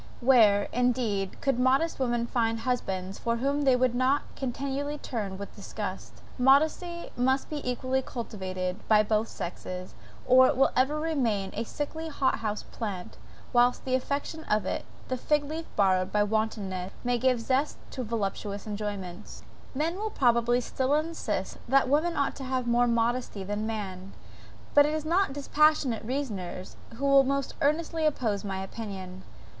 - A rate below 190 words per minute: Yes, average, 160 wpm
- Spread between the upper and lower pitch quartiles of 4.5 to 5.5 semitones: Yes, average, 5.0 semitones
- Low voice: No, high, 245 Hz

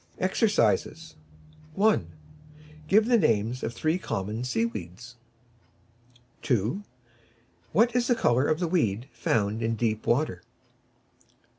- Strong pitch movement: Yes, wide, 8.7 semitones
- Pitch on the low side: Yes, low, 120 Hz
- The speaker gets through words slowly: Yes, slow, 115 wpm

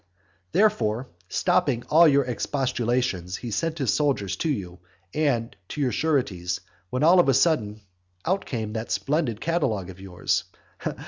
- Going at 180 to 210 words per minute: No, average, 145 wpm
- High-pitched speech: No, low, 125 Hz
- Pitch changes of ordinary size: No, wide, 6.0 semitones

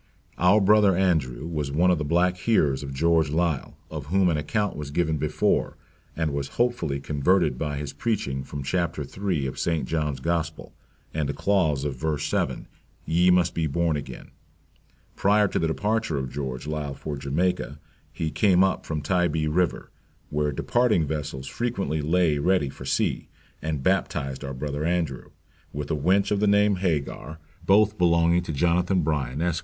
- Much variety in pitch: No, average, 3.9 semitones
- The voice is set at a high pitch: No, very low, 80 Hz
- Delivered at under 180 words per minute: Yes, average, 170 wpm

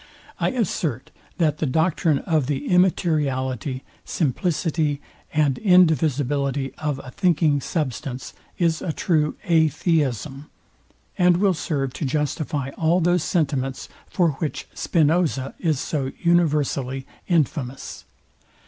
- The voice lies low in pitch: No, medium, 150 Hz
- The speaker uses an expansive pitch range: No, average, 3.7 semitones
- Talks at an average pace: No, slow, 110 wpm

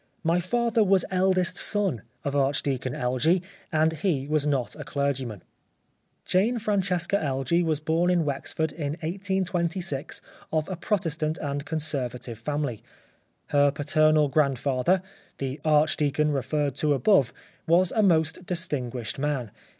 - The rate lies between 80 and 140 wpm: Yes, slow, 135 wpm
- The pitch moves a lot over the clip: No, average, 4.2 semitones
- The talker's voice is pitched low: No, medium, 155 Hz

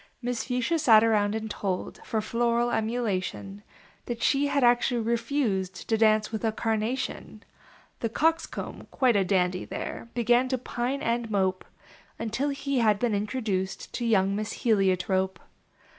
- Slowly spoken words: No, average, 145 wpm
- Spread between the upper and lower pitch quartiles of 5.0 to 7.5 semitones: No, average, 3.1 semitones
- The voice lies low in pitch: No, high, 225 Hz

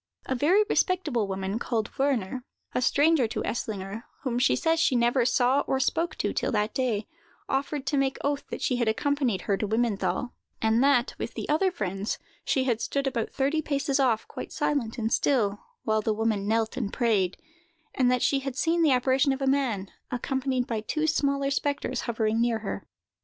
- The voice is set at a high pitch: Yes, very high, 250 Hz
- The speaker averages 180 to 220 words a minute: Yes, average, 185 wpm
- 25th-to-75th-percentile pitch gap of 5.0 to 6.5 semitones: No, average, 3.9 semitones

